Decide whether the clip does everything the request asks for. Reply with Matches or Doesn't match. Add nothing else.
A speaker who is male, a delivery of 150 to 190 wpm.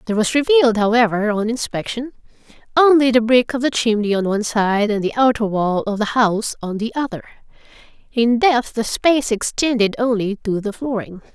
Doesn't match